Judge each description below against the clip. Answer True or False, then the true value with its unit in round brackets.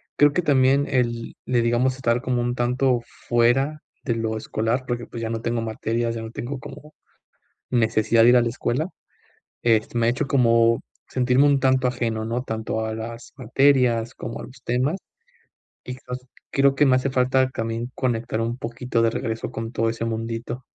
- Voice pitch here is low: True (120 Hz)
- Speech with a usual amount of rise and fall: False (2.2 semitones)